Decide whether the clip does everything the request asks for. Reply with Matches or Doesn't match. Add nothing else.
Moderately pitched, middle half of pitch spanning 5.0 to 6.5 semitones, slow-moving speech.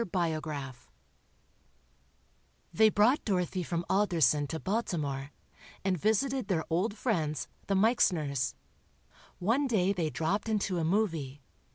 Matches